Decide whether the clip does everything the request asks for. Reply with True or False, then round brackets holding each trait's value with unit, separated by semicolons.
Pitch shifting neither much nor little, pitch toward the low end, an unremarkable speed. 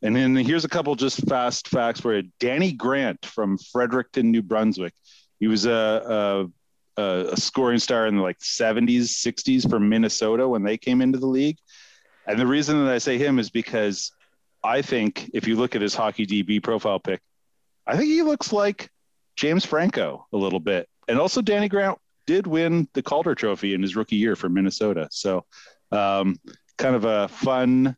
True (4.2 semitones; 120 Hz; 185 wpm)